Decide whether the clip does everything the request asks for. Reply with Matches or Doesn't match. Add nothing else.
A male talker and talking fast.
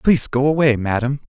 Doesn't match